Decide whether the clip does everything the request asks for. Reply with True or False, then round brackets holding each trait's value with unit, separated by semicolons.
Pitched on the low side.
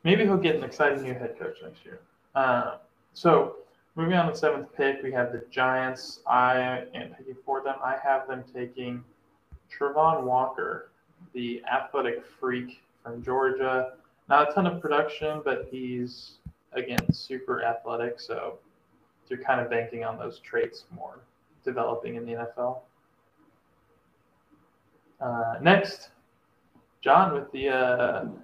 True (130 Hz)